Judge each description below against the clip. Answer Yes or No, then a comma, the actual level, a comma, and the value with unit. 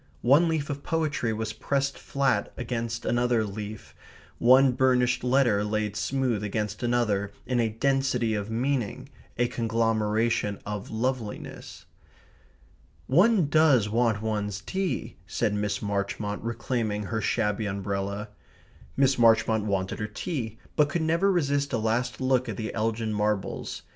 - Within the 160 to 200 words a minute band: No, slow, 135 wpm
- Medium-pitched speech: No, low, 115 Hz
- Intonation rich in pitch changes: No, average, 3.8 semitones